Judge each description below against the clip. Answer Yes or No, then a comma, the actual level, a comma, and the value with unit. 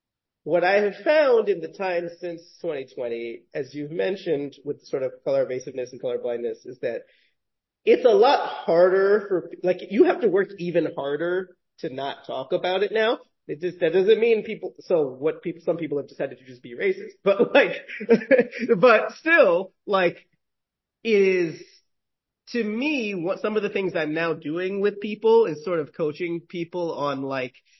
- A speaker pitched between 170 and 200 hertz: Yes, high, 190 Hz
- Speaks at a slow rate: No, average, 180 wpm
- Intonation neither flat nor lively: No, wide, 8.9 semitones